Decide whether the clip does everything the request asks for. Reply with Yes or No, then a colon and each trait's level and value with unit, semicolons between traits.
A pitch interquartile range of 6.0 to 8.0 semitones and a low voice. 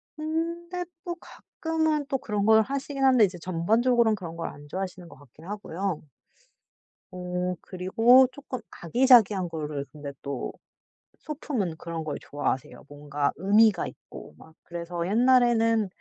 No: wide, 7.3 semitones; high, 200 Hz